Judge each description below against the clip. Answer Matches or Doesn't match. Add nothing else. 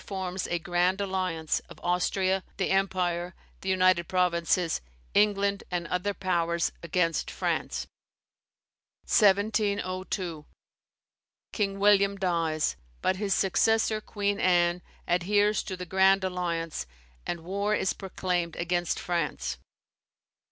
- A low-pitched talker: Doesn't match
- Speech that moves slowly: Matches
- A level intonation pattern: Matches